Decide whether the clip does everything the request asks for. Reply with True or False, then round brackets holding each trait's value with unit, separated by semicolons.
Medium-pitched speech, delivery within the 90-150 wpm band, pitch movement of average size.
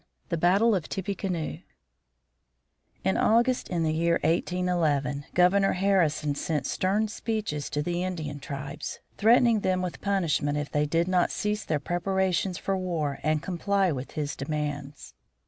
True (175 Hz; 145 wpm; 4.5 semitones)